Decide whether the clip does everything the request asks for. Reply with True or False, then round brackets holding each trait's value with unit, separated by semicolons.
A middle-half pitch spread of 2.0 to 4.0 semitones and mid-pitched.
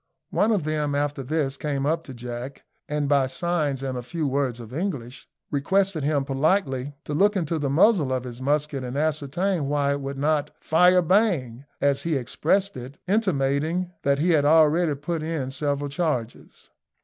True (3.3 semitones; 145 Hz)